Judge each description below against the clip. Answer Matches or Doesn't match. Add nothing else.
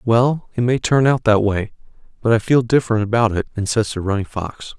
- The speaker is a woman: Doesn't match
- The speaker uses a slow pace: Doesn't match